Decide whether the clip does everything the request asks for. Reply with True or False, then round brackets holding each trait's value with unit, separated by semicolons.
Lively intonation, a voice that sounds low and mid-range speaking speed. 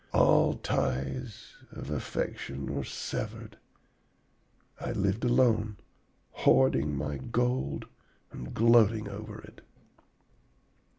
False (8.6 semitones; 100 Hz; 85 wpm)